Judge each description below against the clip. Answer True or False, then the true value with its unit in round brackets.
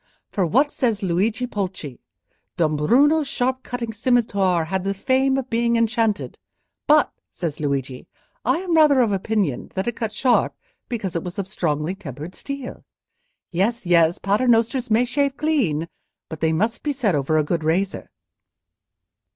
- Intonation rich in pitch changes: True (6.7 semitones)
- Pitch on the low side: False (210 Hz)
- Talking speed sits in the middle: True (150 wpm)